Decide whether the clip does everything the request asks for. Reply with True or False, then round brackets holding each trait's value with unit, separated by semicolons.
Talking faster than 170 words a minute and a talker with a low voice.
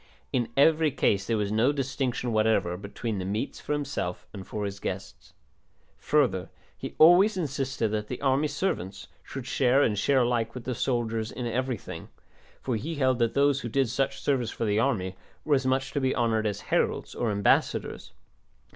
True (180 wpm; 120 Hz)